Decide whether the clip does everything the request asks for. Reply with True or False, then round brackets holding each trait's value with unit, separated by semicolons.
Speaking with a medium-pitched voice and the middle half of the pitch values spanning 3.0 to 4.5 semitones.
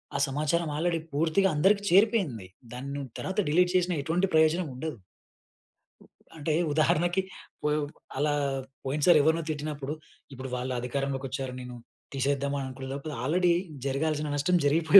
True (150 Hz; 3.6 semitones)